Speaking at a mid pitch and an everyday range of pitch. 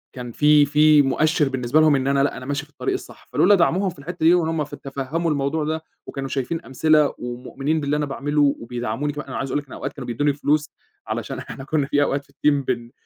No: medium, 145 Hz; narrow, 2.2 semitones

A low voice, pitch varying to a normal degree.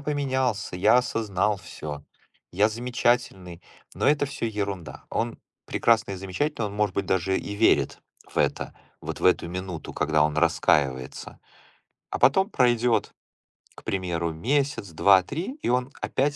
No: low, 105 Hz; wide, 5.7 semitones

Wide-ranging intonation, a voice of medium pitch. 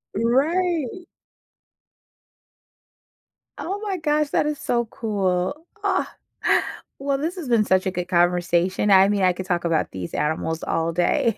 No: wide, 9.0 semitones; high, 205 Hz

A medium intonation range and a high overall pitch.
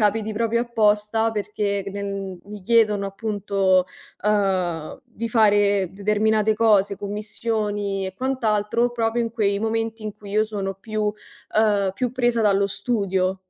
No: narrow, 2.0 semitones; high, 210 Hz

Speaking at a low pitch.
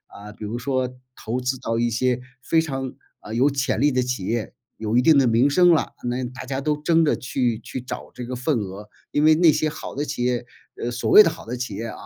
Yes: low, 125 Hz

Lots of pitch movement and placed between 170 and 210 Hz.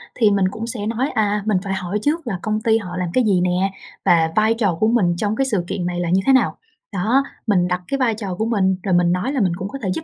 No: average, 3.9 semitones; high, 205 Hz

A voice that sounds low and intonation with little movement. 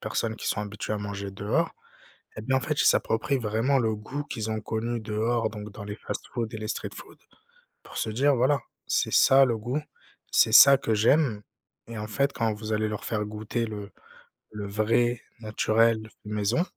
Yes: low, 110 Hz; narrow, 2.3 semitones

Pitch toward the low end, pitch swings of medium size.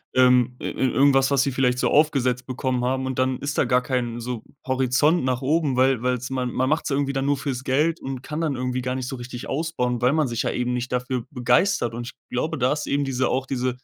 No: low, 130 Hz; narrow, 1.6 semitones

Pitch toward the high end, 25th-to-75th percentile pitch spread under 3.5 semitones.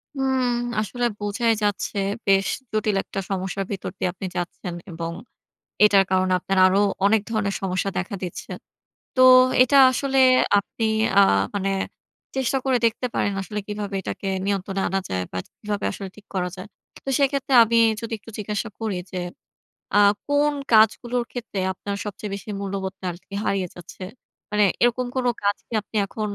Yes: high, 205 Hz; average, 3.0 semitones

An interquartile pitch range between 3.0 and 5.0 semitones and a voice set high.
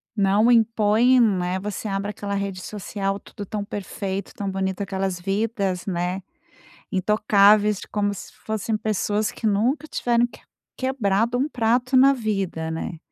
No: narrow, 2.5 semitones; high, 205 Hz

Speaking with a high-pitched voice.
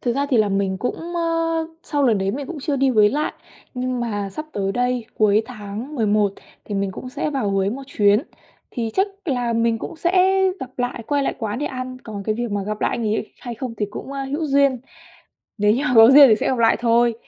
Yes: high, 240 Hz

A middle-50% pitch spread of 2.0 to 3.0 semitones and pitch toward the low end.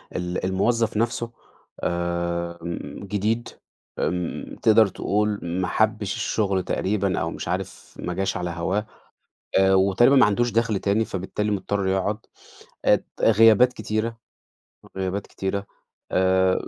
Yes: average, 2.7 semitones; low, 100 Hz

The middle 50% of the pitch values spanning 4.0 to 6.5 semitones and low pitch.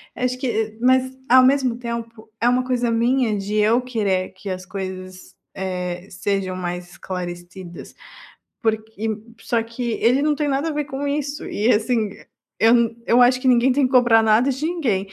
No: average, 4.5 semitones; high, 230 Hz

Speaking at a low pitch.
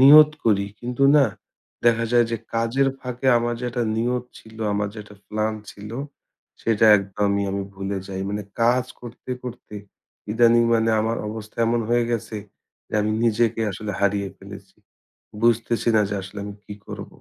Yes: low, 115 Hz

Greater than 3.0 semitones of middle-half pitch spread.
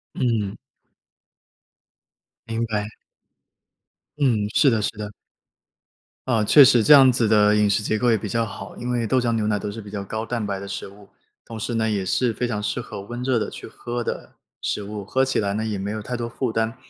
No: narrow, 2.5 semitones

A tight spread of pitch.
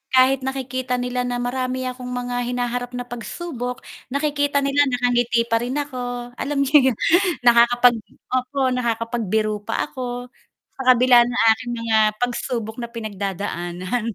Yes: narrow, 1.5 semitones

